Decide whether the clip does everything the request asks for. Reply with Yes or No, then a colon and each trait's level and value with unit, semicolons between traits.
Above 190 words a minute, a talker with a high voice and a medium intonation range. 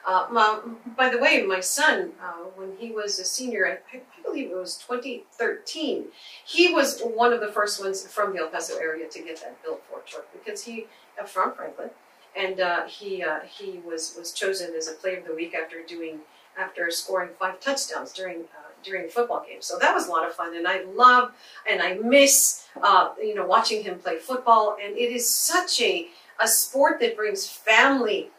No: fast, 205 wpm; high, 225 Hz; wide, 7.1 semitones